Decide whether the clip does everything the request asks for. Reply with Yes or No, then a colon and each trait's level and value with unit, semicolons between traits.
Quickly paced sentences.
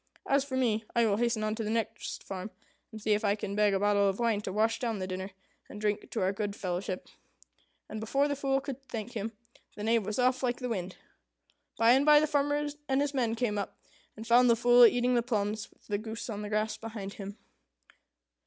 Yes: fast, 230 wpm